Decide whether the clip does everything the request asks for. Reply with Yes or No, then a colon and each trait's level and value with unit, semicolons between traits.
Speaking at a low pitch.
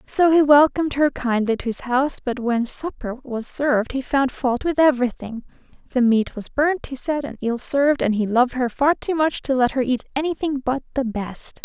No: very high, 260 Hz